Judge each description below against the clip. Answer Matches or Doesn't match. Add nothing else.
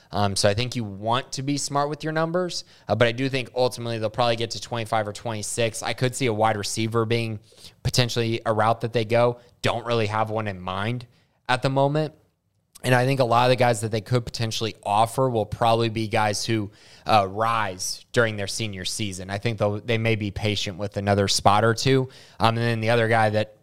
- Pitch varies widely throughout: Doesn't match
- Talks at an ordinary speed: Doesn't match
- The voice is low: Matches